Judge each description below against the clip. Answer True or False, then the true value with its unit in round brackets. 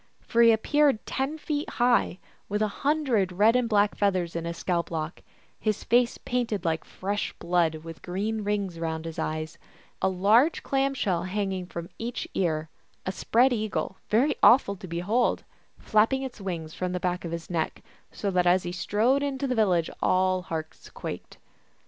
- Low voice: False (200 Hz)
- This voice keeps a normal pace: True (175 wpm)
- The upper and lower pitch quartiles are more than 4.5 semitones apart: True (5.2 semitones)